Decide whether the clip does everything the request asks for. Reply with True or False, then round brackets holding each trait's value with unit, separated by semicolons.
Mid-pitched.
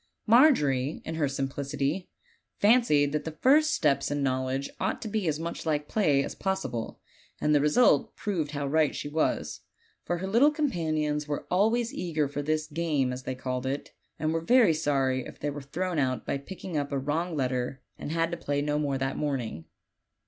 True (150 Hz)